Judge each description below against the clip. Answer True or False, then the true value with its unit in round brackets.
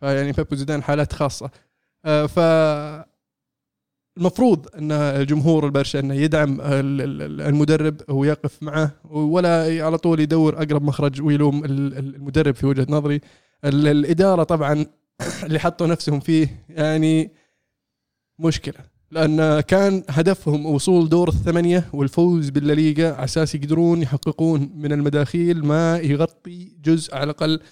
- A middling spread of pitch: False (2.1 semitones)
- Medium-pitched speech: True (150 Hz)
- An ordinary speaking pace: True (115 wpm)